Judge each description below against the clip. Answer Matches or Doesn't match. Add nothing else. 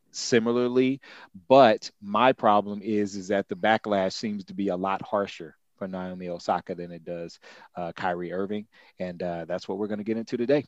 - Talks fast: Doesn't match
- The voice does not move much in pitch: Doesn't match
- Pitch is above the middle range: Doesn't match